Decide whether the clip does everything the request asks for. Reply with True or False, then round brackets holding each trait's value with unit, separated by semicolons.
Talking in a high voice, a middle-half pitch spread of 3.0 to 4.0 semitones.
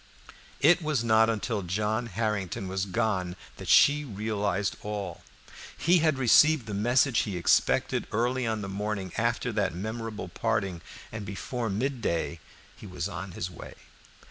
False (105 Hz; 3.5 semitones)